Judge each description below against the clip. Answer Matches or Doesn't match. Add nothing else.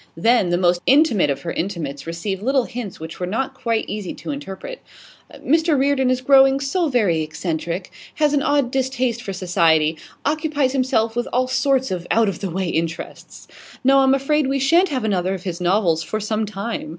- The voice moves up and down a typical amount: Doesn't match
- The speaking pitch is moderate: Doesn't match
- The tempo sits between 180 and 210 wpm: Matches